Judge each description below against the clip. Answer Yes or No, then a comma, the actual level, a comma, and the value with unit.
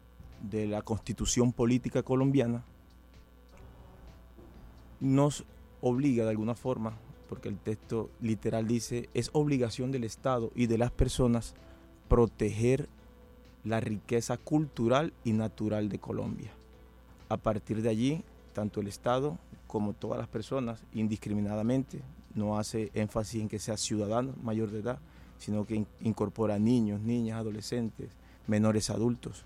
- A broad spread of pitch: No, narrow, 2.5 semitones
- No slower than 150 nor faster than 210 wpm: No, slow, 125 wpm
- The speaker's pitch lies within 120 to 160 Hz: No, low, 110 Hz